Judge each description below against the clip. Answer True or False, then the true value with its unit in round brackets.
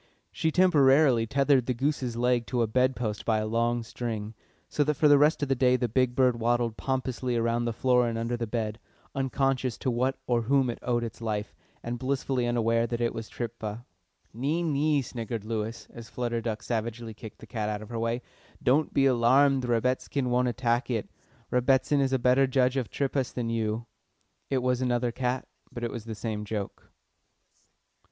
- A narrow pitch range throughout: True (2.3 semitones)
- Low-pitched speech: True (120 Hz)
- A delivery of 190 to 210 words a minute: True (195 wpm)